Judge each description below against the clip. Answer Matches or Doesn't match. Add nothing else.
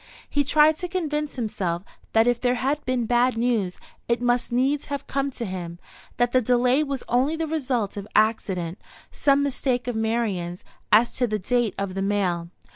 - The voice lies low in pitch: Doesn't match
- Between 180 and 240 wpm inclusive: Matches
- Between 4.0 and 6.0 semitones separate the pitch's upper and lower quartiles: Matches